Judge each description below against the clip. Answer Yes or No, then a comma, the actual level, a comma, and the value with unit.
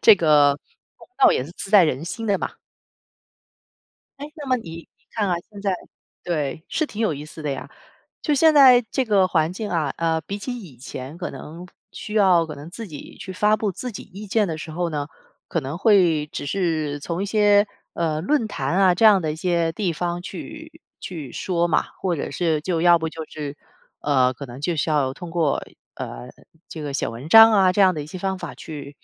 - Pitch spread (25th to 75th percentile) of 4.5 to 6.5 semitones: Yes, average, 5.0 semitones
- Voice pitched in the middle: Yes, medium, 170 Hz